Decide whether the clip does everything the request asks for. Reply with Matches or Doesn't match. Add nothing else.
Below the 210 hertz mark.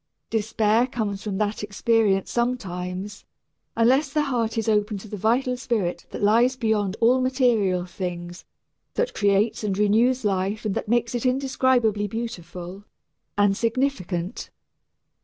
Doesn't match